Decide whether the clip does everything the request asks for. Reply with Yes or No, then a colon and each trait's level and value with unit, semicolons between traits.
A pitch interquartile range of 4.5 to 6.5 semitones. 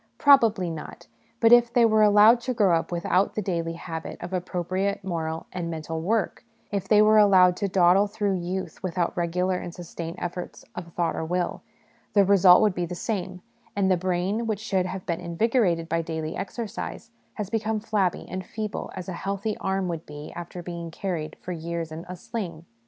No: average, 3.3 semitones